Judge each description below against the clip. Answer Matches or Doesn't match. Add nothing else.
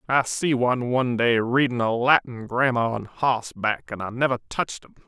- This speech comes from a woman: Doesn't match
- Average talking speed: Matches